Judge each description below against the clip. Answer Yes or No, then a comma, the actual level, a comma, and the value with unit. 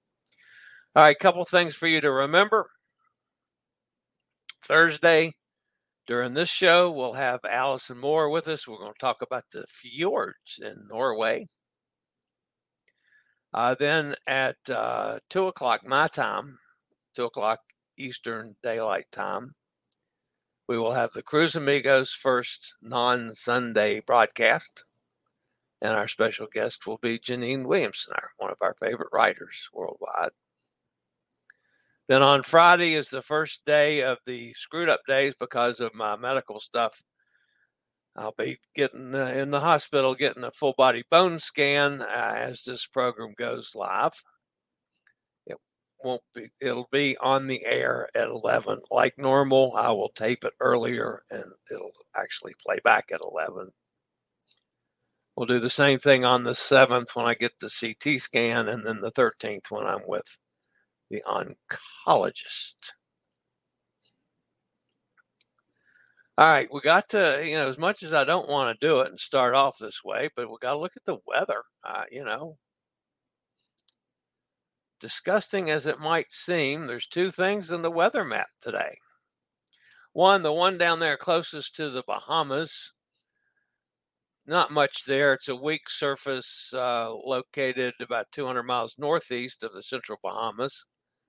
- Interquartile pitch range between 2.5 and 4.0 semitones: No, average, 4.7 semitones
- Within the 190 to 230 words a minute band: No, average, 145 wpm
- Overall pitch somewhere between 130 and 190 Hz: Yes, medium, 140 Hz